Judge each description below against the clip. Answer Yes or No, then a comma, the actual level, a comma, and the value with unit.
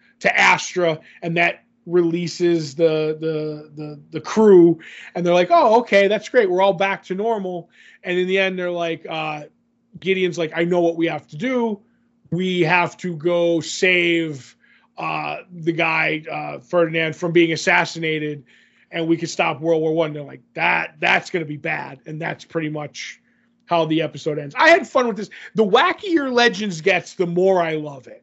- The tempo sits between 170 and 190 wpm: Yes, average, 185 wpm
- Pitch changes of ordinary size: Yes, average, 3.4 semitones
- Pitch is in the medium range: Yes, medium, 170 Hz